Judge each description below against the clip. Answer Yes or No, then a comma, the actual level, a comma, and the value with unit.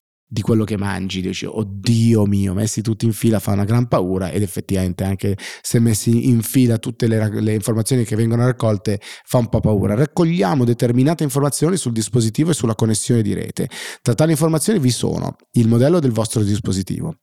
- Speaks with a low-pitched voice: Yes, low, 115 Hz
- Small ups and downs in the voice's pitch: No, average, 3.3 semitones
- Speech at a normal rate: No, fast, 185 wpm